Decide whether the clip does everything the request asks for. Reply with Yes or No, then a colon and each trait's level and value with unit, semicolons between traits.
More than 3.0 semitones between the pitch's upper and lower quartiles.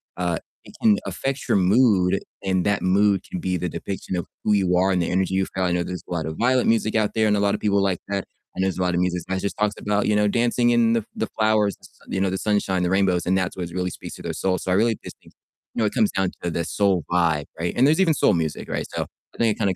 No: average, 2.7 semitones